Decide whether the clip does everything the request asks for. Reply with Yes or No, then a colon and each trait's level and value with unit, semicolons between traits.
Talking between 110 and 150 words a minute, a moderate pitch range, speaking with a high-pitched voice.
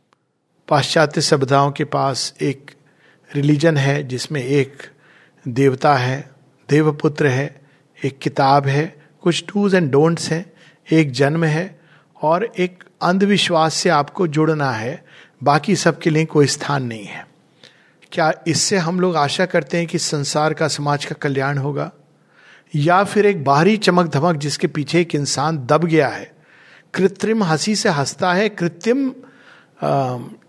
No: average, 140 wpm; average, 3.4 semitones; medium, 155 Hz